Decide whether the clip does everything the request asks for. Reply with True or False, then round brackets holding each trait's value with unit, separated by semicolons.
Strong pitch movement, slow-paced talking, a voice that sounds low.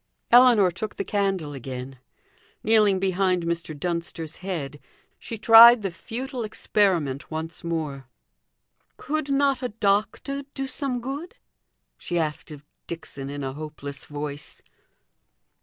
False (7.1 semitones; 125 wpm; 185 Hz)